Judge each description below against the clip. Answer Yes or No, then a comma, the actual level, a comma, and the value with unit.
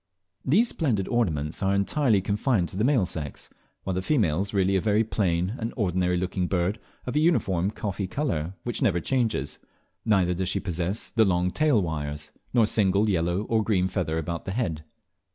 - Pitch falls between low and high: No, very low, 95 Hz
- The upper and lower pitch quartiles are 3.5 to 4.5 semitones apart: Yes, average, 4.1 semitones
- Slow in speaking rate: No, average, 190 wpm